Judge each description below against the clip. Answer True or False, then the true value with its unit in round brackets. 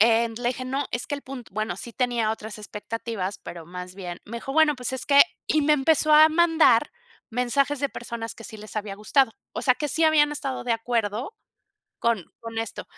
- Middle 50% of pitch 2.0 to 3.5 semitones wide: False (4.3 semitones)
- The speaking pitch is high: True (240 Hz)